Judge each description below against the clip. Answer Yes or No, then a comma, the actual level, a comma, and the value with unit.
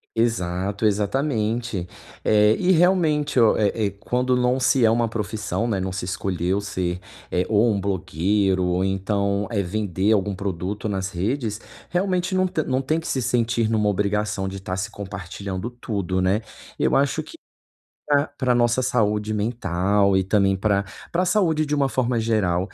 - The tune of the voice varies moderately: Yes, average, 4.2 semitones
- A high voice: No, low, 105 Hz